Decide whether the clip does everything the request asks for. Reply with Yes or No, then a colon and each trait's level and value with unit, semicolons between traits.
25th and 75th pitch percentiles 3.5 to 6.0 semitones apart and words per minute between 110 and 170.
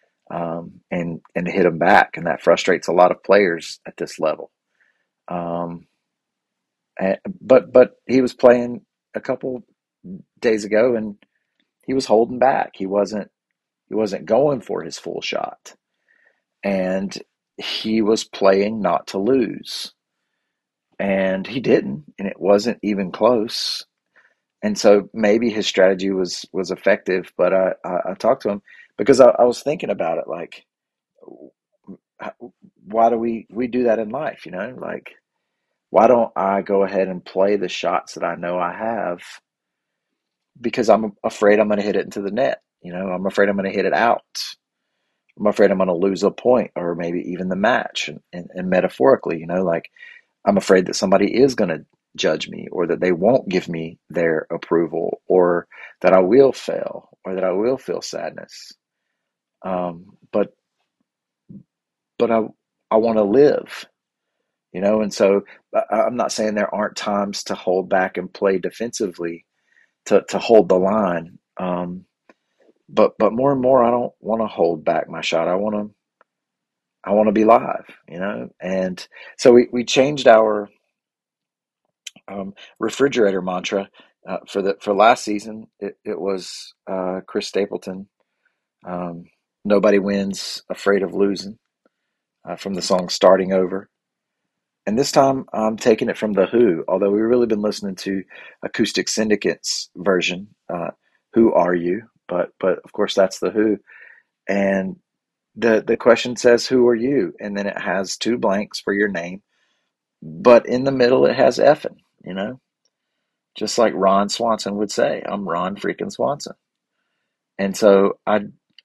No: average, 3.0 semitones; average, 165 wpm